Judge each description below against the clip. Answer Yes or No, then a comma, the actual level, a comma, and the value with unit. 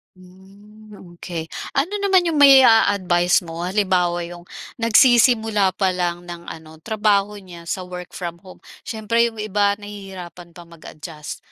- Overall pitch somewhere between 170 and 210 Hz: Yes, high, 190 Hz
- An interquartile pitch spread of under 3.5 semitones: No, average, 3.8 semitones